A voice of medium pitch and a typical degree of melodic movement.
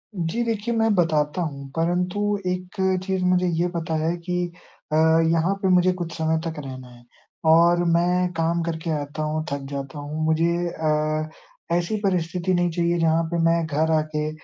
No: medium, 165 Hz; narrow, 2.3 semitones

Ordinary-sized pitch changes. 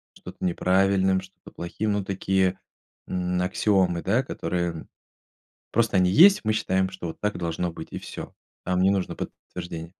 No: narrow, 1.7 semitones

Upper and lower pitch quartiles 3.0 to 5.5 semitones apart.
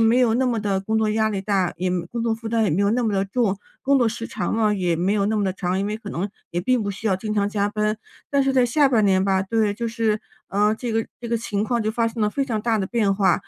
No: narrow, 2.5 semitones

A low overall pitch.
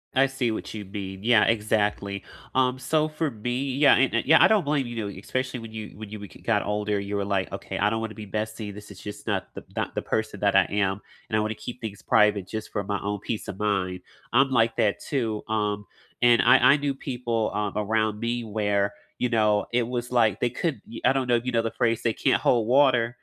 Yes: low, 110 Hz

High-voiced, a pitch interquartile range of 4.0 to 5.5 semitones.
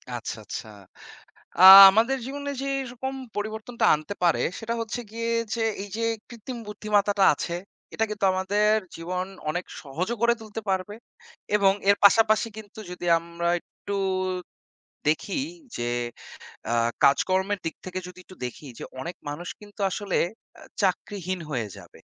No: high, 200 Hz; average, 3.6 semitones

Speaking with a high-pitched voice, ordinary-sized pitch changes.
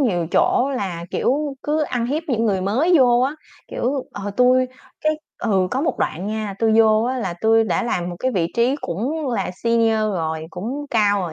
Yes: high, 230 Hz; average, 4.6 semitones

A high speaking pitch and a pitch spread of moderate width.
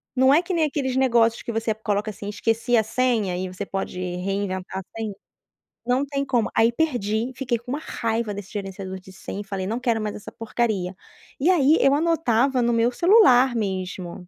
Yes: high, 225 Hz; average, 4.5 semitones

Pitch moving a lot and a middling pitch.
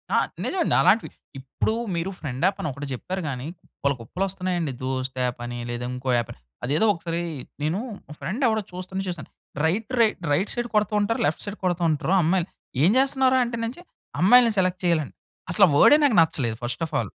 Yes: wide, 6.8 semitones; medium, 175 Hz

